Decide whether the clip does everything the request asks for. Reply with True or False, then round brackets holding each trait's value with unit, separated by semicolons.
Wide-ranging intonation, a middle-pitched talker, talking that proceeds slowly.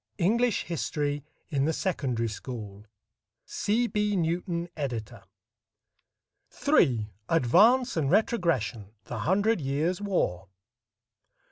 True (8.2 semitones; 160 Hz; 95 wpm)